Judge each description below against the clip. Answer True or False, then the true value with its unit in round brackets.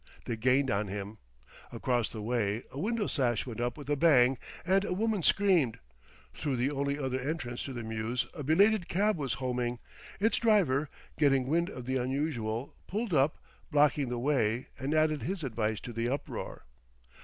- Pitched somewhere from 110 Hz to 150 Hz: True (135 Hz)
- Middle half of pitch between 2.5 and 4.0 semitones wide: False (4.7 semitones)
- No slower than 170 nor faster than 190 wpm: True (180 wpm)